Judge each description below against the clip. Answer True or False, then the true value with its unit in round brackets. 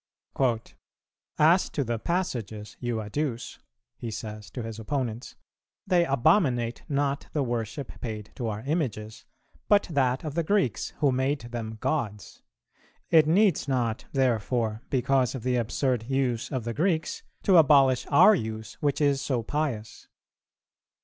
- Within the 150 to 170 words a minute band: False (140 wpm)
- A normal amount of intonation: True (4.6 semitones)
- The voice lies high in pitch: False (130 Hz)